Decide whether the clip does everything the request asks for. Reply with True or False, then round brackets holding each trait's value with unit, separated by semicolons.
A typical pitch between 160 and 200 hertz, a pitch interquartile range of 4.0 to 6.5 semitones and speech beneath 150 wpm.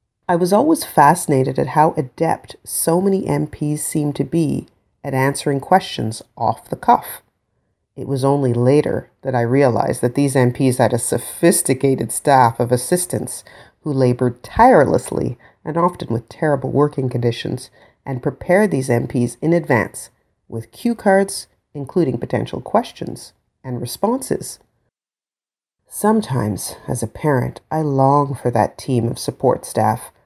False (135 Hz; 4.3 semitones; 140 wpm)